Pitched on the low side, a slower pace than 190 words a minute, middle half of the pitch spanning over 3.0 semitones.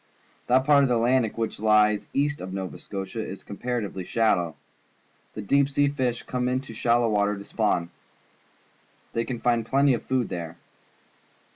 Yes: low, 115 Hz; average, 170 wpm; average, 4.0 semitones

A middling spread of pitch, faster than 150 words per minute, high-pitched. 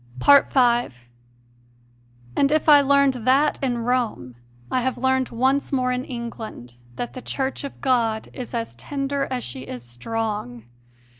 No: average, 3.1 semitones; average, 145 wpm; very high, 250 Hz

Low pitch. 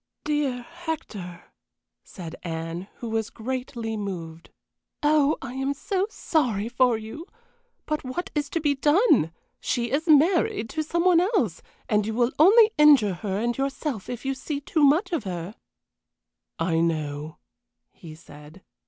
No: very high, 250 Hz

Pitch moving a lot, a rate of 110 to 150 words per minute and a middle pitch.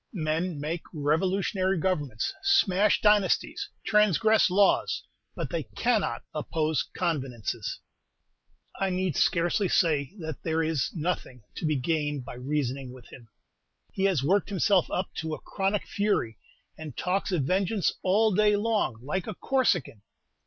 No: average, 5.0 semitones; average, 140 wpm; medium, 175 Hz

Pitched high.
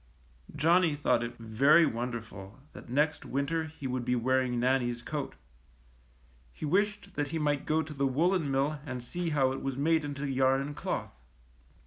No: medium, 140 Hz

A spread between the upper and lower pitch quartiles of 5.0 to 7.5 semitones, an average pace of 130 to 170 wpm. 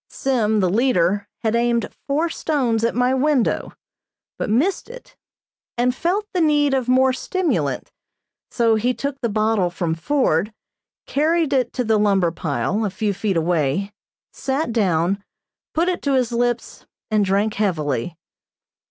Yes: wide, 5.4 semitones; average, 150 wpm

